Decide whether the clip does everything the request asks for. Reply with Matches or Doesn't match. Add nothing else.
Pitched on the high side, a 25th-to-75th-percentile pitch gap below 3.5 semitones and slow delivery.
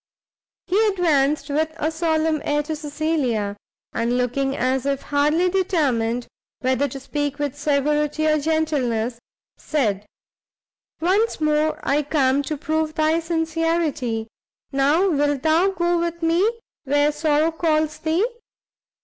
Matches